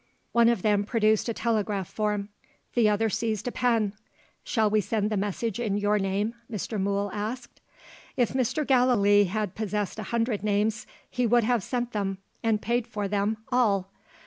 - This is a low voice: No, high, 215 Hz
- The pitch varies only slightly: Yes, narrow, 2.3 semitones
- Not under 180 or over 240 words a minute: No, average, 170 wpm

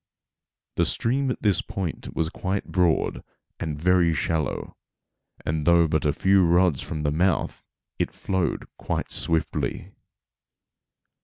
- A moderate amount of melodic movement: Yes, average, 3.0 semitones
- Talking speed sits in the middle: No, slow, 130 wpm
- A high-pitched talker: No, very low, 85 Hz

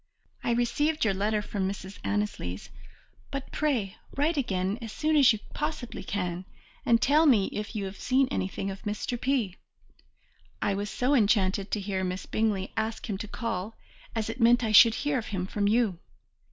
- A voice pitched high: Yes, high, 215 Hz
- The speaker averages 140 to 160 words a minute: No, average, 180 wpm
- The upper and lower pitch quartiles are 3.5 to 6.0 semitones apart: Yes, average, 4.0 semitones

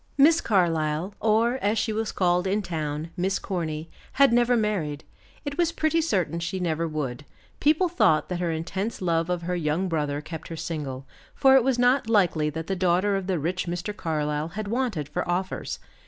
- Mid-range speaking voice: Yes, medium, 180 Hz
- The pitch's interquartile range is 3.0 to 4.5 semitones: No, average, 5.2 semitones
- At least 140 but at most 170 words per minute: No, average, 190 wpm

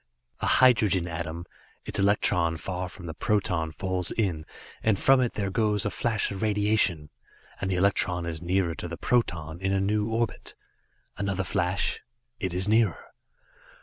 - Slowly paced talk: No, average, 160 wpm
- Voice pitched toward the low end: Yes, very low, 95 Hz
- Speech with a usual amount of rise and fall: Yes, average, 3.4 semitones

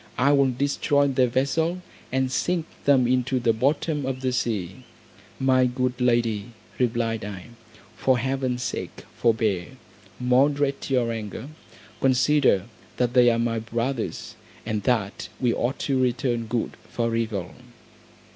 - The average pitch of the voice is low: Yes, low, 125 Hz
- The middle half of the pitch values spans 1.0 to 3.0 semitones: Yes, narrow, 2.5 semitones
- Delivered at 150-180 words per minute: No, slow, 135 wpm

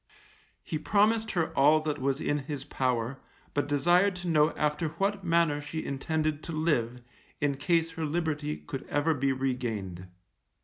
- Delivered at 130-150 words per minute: No, average, 160 wpm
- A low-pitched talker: No, medium, 150 Hz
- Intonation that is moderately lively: Yes, average, 3.3 semitones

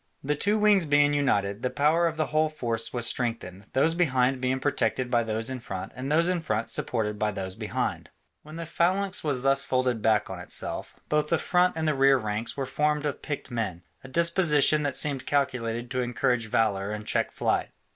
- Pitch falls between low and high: No, low, 130 Hz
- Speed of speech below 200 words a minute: No, fast, 205 wpm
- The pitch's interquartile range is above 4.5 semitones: Yes, average, 5.1 semitones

